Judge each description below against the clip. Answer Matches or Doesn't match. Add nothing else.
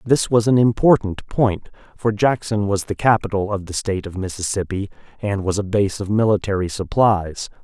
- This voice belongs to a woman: Doesn't match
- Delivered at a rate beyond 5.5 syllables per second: Doesn't match